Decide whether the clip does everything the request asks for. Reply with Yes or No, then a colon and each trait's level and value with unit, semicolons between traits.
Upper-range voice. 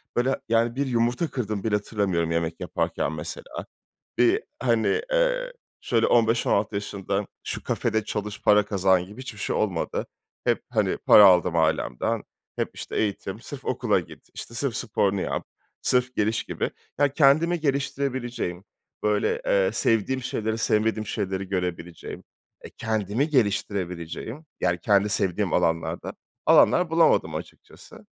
No: low, 110 Hz